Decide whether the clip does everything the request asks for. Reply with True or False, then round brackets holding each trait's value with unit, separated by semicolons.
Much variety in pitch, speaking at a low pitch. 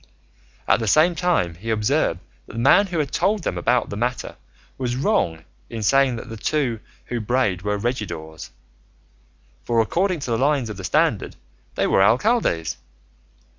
True (6.0 semitones; 120 Hz)